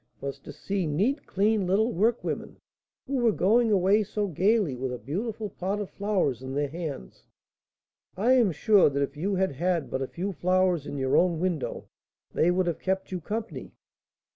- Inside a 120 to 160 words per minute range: No, average, 185 wpm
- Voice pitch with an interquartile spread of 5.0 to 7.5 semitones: Yes, wide, 5.6 semitones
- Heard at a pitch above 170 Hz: Yes, medium, 185 Hz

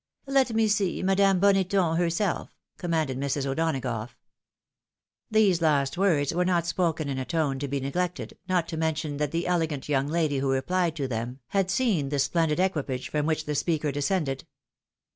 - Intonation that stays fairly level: No, average, 4.4 semitones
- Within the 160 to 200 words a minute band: Yes, average, 175 wpm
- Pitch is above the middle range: No, medium, 160 Hz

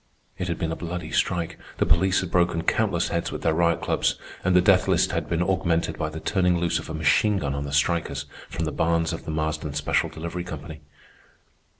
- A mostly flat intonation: Yes, narrow, 2.3 semitones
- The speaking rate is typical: No, fast, 220 wpm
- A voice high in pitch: No, very low, 85 Hz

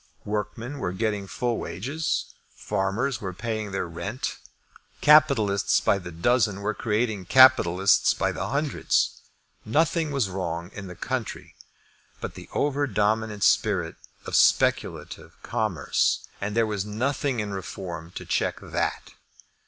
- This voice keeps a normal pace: No, slow, 130 wpm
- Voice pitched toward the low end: Yes, low, 105 Hz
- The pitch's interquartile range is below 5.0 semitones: Yes, average, 4.2 semitones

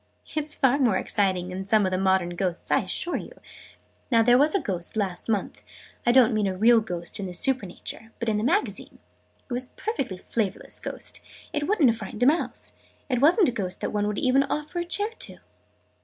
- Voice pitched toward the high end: Yes, high, 225 Hz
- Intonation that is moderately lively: No, wide, 6.2 semitones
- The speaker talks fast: Yes, fast, 215 wpm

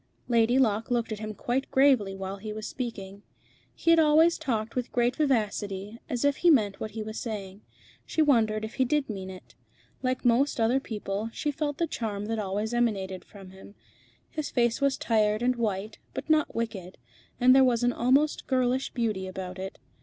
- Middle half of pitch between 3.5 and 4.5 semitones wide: Yes, average, 4.0 semitones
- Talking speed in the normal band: Yes, average, 190 wpm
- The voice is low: No, high, 230 Hz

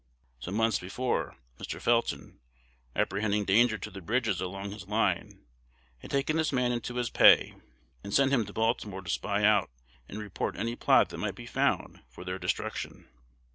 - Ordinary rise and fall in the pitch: Yes, average, 3.5 semitones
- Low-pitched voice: Yes, low, 110 Hz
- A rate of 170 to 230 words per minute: Yes, average, 175 wpm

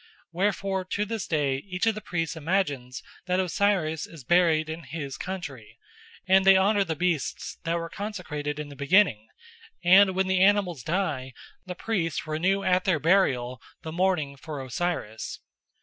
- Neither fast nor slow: Yes, average, 160 wpm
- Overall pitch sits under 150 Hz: No, medium, 175 Hz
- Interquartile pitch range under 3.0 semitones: No, average, 4.4 semitones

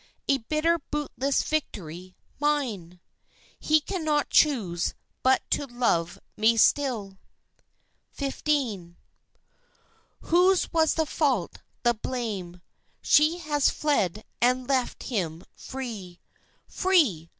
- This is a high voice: Yes, very high, 255 Hz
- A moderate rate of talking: No, slow, 95 wpm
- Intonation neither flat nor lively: No, wide, 7.4 semitones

